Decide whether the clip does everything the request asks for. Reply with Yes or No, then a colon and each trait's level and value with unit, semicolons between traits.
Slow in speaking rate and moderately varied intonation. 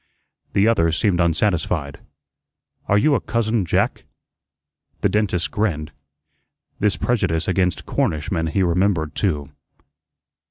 Yes: slow, 110 wpm; average, 4.3 semitones